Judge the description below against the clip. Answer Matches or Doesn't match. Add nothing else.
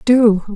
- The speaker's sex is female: Matches